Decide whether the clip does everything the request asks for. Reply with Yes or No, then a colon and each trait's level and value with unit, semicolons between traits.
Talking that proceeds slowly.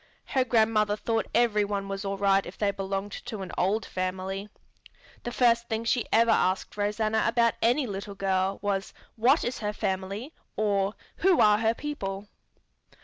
No: average, 165 wpm